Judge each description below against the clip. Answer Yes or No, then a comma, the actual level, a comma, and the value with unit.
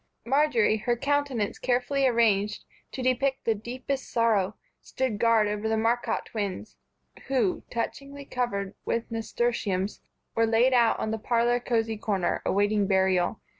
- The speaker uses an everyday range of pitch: Yes, average, 3.0 semitones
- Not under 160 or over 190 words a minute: No, slow, 135 wpm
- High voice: Yes, high, 230 Hz